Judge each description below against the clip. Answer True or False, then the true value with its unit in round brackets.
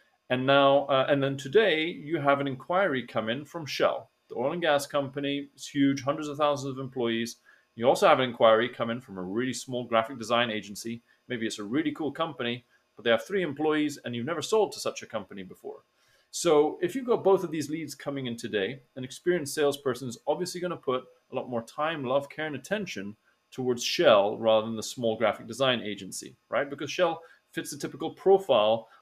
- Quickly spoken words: True (215 wpm)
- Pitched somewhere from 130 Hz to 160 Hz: True (140 Hz)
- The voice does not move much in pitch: False (4.6 semitones)